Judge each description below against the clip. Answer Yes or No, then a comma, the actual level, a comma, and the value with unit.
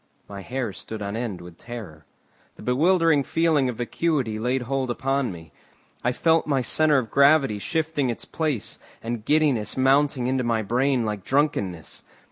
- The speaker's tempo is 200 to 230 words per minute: No, average, 160 wpm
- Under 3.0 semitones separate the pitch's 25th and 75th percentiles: No, average, 4.7 semitones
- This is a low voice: Yes, low, 125 Hz